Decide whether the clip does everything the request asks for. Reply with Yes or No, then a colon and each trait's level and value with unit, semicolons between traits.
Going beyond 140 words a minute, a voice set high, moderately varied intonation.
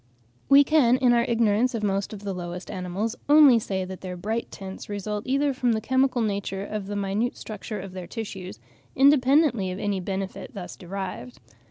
Yes: average, 185 wpm; high, 205 Hz; average, 4.2 semitones